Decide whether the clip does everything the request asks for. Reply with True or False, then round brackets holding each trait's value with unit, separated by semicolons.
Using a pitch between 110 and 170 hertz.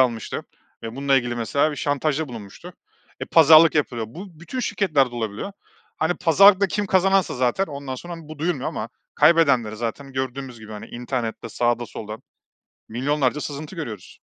True (140 Hz)